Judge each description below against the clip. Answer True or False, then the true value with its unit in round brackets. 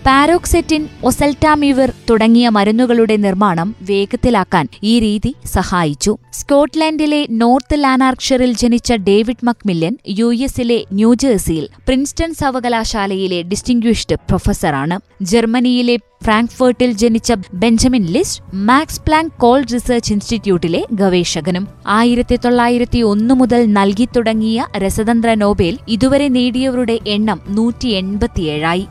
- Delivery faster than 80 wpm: True (95 wpm)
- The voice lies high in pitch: True (235 Hz)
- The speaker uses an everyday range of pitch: True (3.7 semitones)